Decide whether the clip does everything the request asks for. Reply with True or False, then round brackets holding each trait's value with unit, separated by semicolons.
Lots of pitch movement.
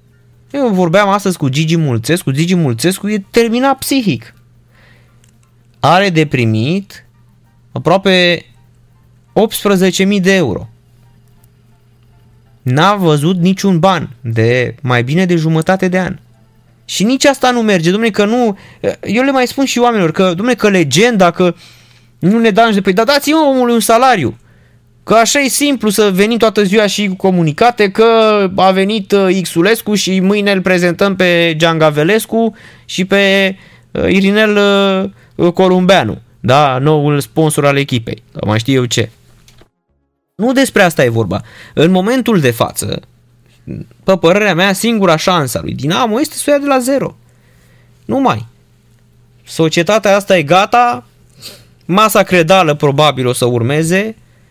True (8.9 semitones)